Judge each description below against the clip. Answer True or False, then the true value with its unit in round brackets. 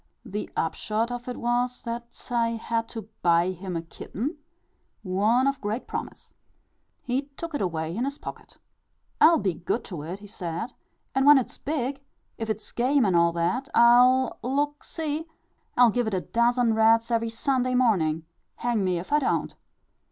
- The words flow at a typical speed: True (175 wpm)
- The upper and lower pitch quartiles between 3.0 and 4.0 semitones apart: False (4.7 semitones)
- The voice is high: True (235 Hz)